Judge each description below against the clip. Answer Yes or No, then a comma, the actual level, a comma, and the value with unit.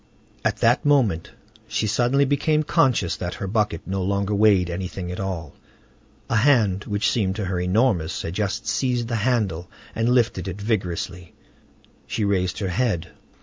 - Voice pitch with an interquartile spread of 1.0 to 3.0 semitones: No, average, 4.5 semitones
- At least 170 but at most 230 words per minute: No, average, 160 wpm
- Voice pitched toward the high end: No, low, 100 Hz